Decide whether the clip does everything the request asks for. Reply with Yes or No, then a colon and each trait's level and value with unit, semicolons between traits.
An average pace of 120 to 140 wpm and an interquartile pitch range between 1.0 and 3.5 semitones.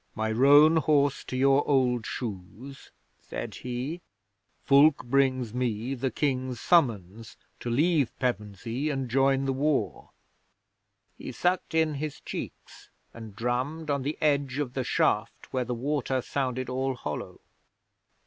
Yes: slow, 135 wpm; average, 2.7 semitones